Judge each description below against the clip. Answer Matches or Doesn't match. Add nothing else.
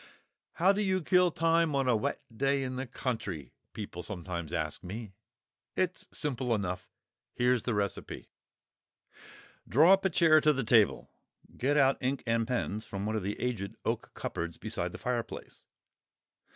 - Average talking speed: Matches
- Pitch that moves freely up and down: Matches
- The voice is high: Doesn't match